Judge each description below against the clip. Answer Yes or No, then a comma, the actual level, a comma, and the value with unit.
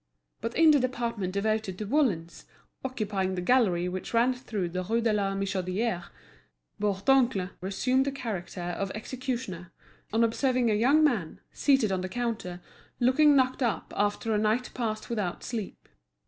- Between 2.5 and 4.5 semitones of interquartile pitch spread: No, average, 5.0 semitones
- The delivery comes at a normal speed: Yes, average, 160 wpm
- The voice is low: No, high, 220 Hz